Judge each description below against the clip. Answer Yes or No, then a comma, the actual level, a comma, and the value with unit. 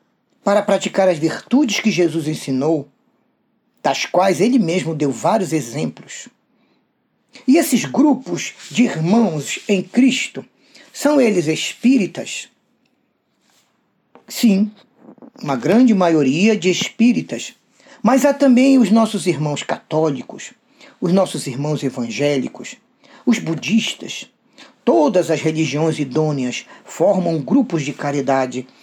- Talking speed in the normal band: No, slow, 105 wpm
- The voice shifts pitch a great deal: Yes, wide, 7.7 semitones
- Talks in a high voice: Yes, high, 200 Hz